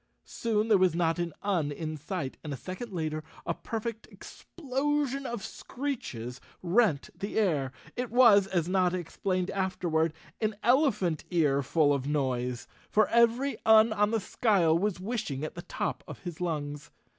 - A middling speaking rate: Yes, average, 160 wpm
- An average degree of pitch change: No, wide, 6.2 semitones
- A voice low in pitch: No, medium, 185 Hz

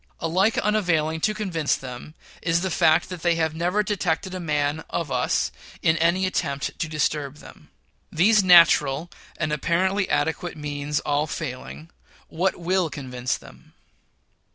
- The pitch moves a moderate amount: Yes, average, 3.5 semitones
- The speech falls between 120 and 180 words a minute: Yes, average, 145 wpm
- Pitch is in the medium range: Yes, medium, 160 Hz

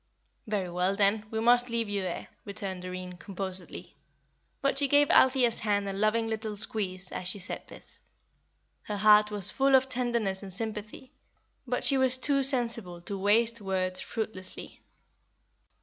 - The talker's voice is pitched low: No, high, 210 Hz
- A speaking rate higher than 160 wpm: No, average, 155 wpm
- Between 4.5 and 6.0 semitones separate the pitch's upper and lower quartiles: No, average, 3.8 semitones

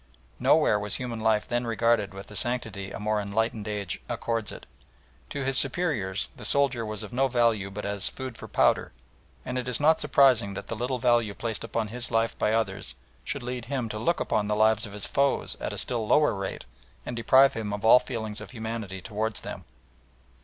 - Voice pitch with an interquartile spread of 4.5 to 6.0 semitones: No, average, 3.0 semitones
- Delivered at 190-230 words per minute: Yes, fast, 205 wpm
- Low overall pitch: Yes, low, 115 Hz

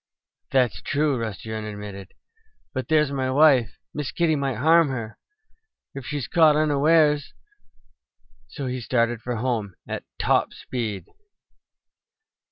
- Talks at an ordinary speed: No, slow, 130 wpm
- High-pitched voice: No, low, 130 Hz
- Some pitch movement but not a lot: Yes, average, 4.9 semitones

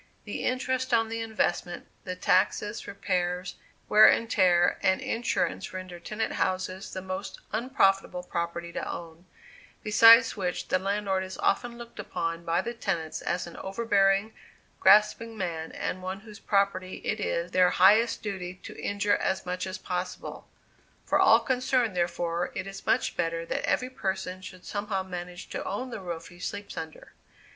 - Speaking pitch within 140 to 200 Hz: Yes, high, 190 Hz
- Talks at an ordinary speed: Yes, average, 160 wpm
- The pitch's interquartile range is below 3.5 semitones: Yes, average, 3.0 semitones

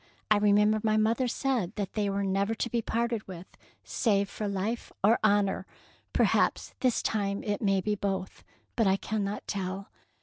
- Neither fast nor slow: Yes, average, 175 wpm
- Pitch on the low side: No, high, 205 Hz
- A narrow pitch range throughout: Yes, narrow, 1.9 semitones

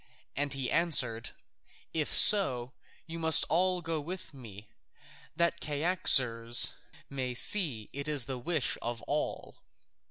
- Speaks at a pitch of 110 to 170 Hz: Yes, medium, 140 Hz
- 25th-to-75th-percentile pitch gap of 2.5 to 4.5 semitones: No, average, 5.3 semitones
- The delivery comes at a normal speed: No, slow, 125 wpm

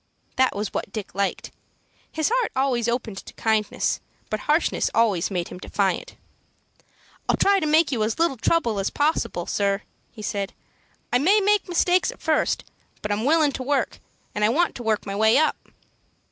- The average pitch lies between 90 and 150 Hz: No, high, 235 Hz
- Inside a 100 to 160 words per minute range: No, average, 180 wpm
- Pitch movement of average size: No, wide, 7.0 semitones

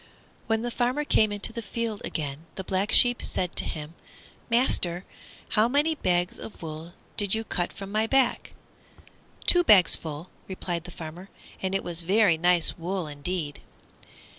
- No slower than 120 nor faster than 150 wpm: No, average, 165 wpm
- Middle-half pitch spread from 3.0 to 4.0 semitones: No, average, 4.7 semitones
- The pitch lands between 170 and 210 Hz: Yes, high, 190 Hz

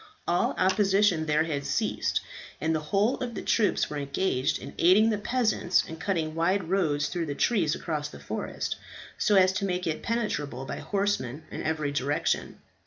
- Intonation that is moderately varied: Yes, average, 4.9 semitones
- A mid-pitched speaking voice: Yes, medium, 175 Hz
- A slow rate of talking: No, average, 175 wpm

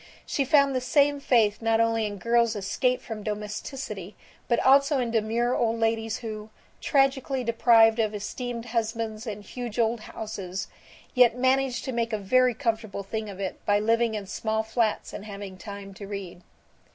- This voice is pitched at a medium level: No, high, 225 Hz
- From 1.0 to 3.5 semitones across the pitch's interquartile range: Yes, narrow, 2.6 semitones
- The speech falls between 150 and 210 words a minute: Yes, average, 170 wpm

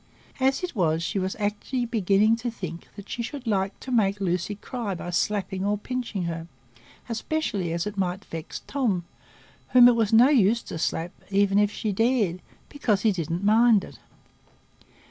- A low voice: No, high, 205 Hz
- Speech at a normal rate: Yes, average, 180 wpm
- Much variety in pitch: No, average, 4.0 semitones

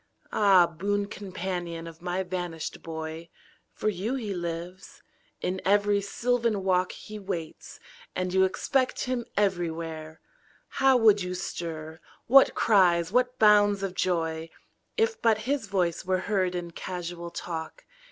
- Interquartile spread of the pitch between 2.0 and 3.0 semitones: No, average, 3.4 semitones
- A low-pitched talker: No, medium, 185 Hz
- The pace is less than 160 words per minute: Yes, slow, 135 wpm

